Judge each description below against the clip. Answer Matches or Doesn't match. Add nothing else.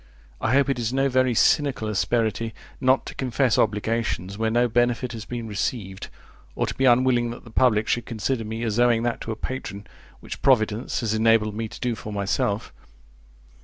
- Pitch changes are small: Matches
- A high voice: Doesn't match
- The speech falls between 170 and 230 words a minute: Matches